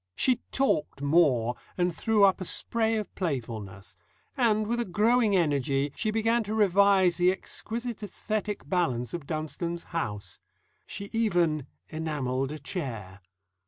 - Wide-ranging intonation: Yes, wide, 7.2 semitones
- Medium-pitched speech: Yes, medium, 175 Hz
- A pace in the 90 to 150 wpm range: Yes, slow, 135 wpm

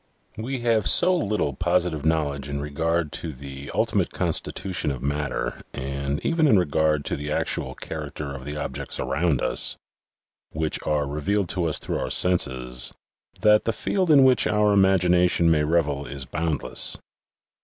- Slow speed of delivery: No, average, 160 wpm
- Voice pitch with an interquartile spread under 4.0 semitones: No, average, 5.0 semitones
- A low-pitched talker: Yes, very low, 80 Hz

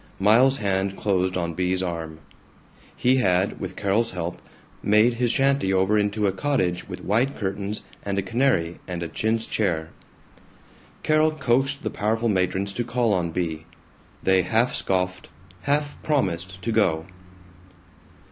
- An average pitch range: Yes, average, 4.4 semitones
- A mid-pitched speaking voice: No, low, 100 Hz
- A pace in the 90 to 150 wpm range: Yes, average, 145 wpm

